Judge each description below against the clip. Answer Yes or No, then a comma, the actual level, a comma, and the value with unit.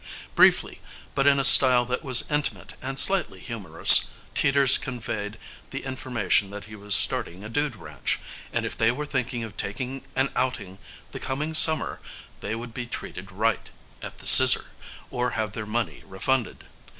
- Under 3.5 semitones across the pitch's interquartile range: No, average, 4.0 semitones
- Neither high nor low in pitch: No, low, 120 Hz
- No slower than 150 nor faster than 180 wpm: Yes, average, 165 wpm